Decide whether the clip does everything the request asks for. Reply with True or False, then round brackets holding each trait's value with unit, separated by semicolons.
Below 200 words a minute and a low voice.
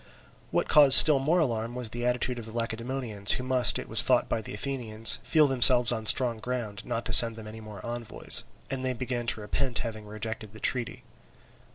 False (205 wpm; 120 Hz)